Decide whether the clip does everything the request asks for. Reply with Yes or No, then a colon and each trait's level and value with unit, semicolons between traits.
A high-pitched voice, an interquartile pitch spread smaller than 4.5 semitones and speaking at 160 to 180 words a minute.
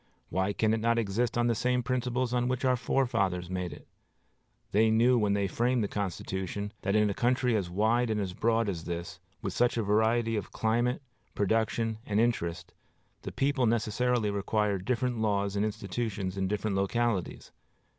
No: low, 110 Hz; average, 3.2 semitones; average, 175 wpm